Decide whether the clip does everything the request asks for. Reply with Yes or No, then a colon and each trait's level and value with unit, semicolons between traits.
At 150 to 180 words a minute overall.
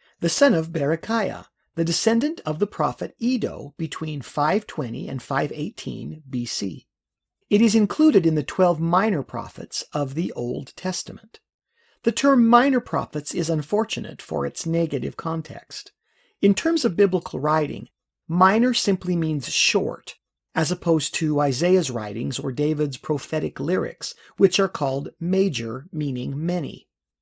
No: slow, 135 wpm